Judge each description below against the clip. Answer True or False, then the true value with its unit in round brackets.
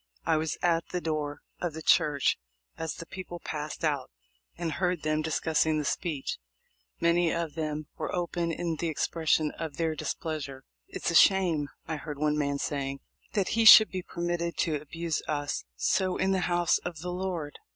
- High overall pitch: False (160 Hz)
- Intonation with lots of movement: False (2.5 semitones)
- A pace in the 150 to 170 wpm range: False (180 wpm)